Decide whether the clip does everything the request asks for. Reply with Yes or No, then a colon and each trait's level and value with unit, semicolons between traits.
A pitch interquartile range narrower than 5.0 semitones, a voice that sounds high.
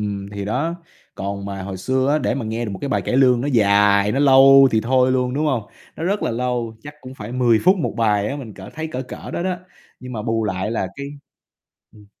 No: average, 4.5 semitones; low, 120 Hz